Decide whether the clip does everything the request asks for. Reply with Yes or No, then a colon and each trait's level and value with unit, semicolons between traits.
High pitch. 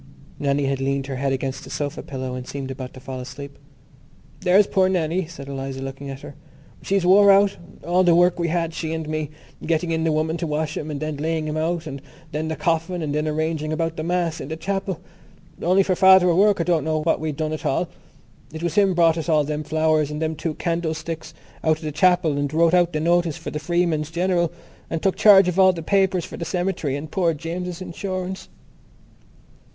No: medium, 160 Hz